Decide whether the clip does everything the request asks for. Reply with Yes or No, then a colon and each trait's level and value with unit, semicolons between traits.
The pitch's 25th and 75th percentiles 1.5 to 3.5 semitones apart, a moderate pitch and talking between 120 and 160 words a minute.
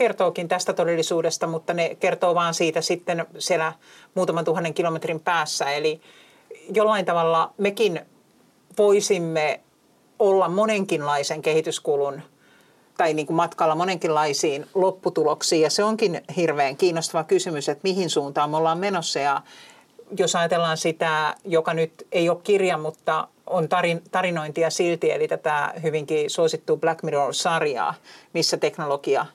Yes: average, 2.7 semitones; medium, 170 Hz; average, 125 wpm